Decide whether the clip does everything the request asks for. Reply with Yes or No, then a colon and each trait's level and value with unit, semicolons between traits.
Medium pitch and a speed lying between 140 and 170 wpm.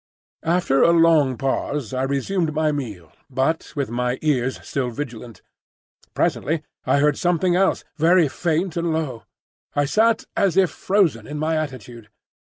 Yes: medium, 150 Hz; average, 150 wpm